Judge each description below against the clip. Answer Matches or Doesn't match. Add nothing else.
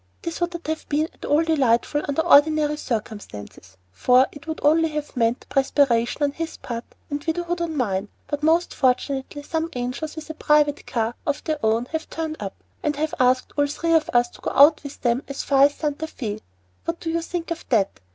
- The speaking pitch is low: Doesn't match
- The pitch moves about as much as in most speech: Matches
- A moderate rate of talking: Doesn't match